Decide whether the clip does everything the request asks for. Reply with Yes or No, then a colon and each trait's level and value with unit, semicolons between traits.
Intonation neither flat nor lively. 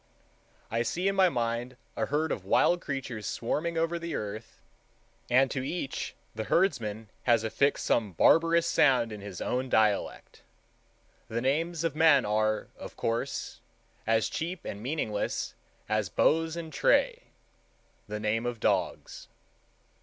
No: wide, 6.8 semitones